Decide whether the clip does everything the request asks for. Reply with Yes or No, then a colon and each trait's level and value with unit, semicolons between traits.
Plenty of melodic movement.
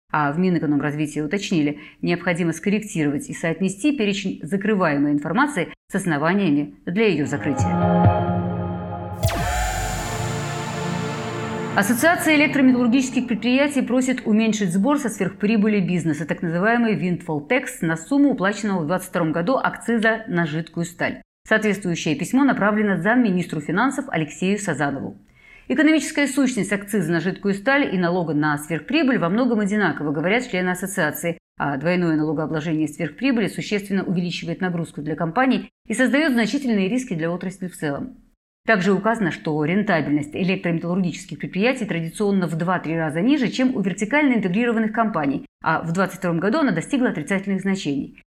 Yes: wide, 5.9 semitones